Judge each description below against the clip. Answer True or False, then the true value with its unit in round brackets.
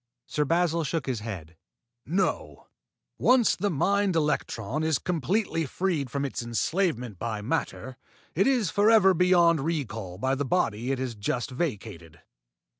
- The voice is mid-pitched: True (145 Hz)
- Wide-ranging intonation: True (7.2 semitones)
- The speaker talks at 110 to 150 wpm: True (145 wpm)